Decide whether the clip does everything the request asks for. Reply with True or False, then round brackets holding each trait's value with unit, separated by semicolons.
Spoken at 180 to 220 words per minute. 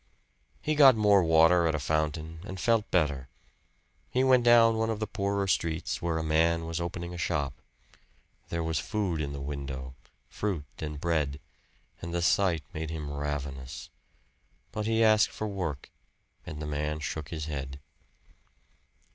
False (160 wpm)